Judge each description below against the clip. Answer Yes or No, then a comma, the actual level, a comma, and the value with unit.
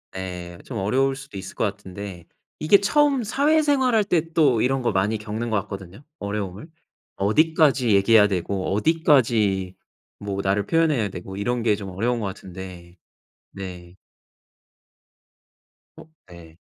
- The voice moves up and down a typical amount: No, wide, 6.3 semitones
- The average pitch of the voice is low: Yes, low, 105 Hz